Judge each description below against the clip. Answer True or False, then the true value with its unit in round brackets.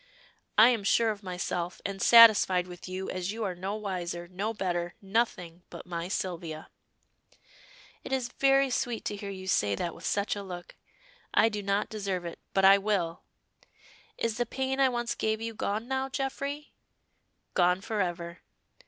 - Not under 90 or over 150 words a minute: False (170 wpm)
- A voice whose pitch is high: True (200 Hz)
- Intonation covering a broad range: False (4.2 semitones)